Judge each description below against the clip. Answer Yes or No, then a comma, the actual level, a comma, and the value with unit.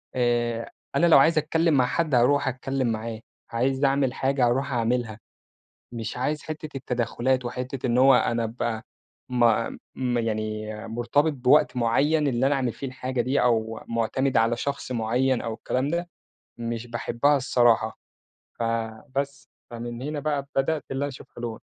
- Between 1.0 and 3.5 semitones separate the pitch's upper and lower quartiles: Yes, average, 2.9 semitones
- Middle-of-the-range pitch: No, low, 125 Hz